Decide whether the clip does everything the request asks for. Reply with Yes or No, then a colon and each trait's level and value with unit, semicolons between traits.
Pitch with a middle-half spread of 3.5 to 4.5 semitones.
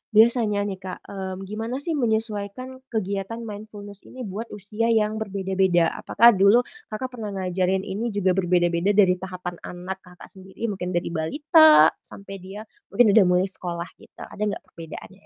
No: average, 3.0 semitones